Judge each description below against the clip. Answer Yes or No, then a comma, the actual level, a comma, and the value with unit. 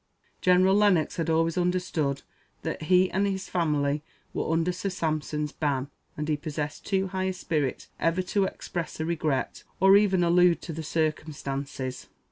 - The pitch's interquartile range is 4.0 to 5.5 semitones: No, average, 3.4 semitones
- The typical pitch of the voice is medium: Yes, medium, 165 Hz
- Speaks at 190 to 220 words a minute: No, average, 160 wpm